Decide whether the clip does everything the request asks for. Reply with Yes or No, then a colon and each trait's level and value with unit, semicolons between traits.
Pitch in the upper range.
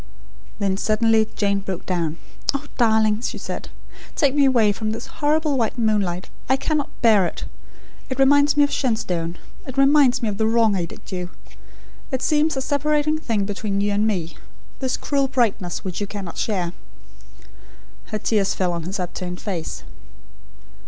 Yes: high, 220 Hz